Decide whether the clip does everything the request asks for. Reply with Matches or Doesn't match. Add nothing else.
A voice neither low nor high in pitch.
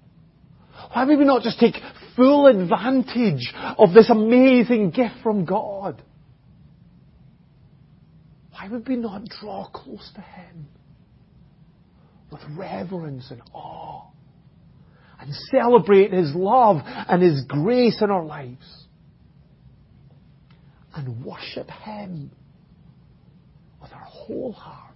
Matches